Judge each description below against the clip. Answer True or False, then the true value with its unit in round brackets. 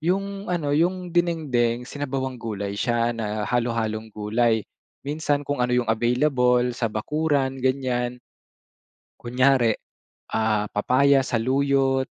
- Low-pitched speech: True (125 Hz)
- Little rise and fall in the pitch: False (3.5 semitones)